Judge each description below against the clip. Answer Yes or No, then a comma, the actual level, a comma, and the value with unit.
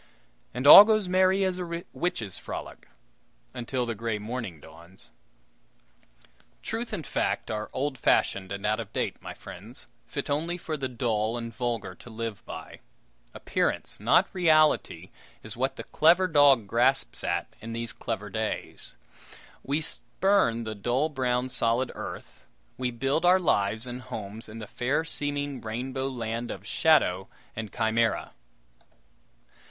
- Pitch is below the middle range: Yes, low, 125 Hz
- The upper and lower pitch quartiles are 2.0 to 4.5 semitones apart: No, average, 5.1 semitones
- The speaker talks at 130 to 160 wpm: Yes, average, 145 wpm